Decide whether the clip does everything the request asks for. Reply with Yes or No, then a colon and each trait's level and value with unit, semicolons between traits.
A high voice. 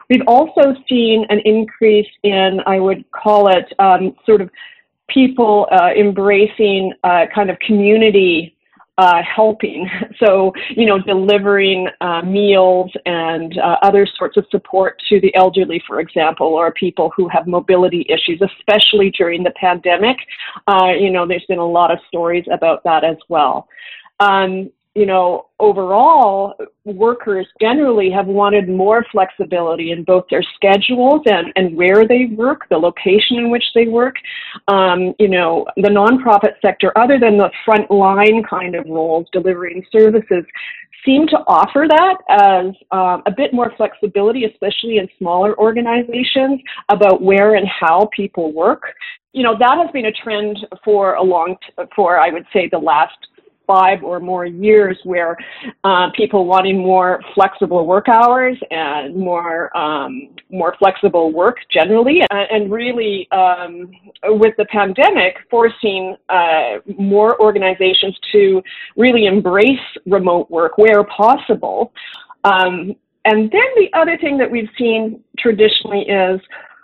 Yes: high, 200 Hz